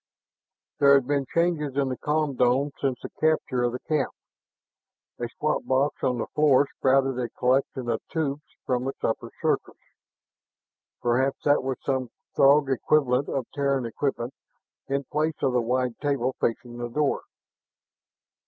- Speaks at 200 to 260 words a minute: No, average, 155 wpm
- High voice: No, low, 135 Hz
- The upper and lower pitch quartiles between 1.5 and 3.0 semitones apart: Yes, narrow, 2.4 semitones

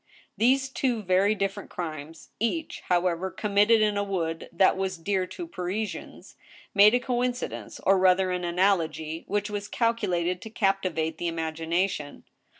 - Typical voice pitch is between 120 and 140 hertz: No, high, 190 Hz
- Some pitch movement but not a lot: Yes, average, 3.6 semitones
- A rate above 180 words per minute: No, average, 150 wpm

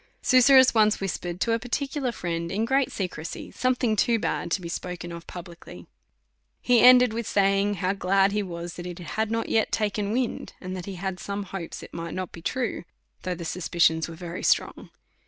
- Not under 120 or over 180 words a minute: No, average, 195 wpm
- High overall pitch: Yes, high, 195 Hz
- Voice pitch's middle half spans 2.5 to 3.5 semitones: No, average, 4.6 semitones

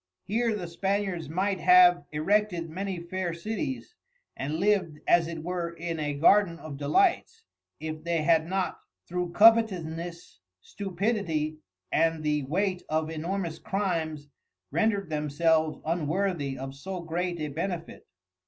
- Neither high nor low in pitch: Yes, medium, 170 Hz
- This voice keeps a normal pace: No, slow, 130 wpm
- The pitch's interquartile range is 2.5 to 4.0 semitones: Yes, average, 3.7 semitones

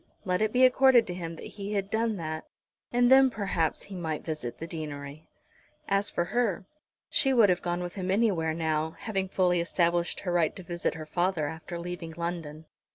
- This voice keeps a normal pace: Yes, average, 195 wpm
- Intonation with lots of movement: No, average, 3.7 semitones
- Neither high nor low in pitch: Yes, medium, 175 Hz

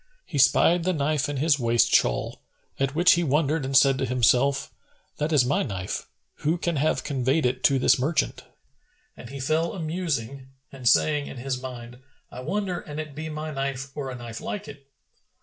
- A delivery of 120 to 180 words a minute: No, average, 195 wpm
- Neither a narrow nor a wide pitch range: Yes, average, 3.3 semitones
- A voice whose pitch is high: No, medium, 140 Hz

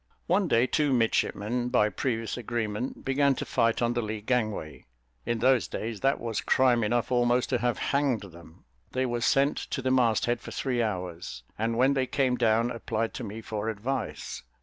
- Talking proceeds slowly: No, average, 190 wpm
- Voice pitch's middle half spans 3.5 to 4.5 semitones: No, average, 2.8 semitones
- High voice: No, low, 120 Hz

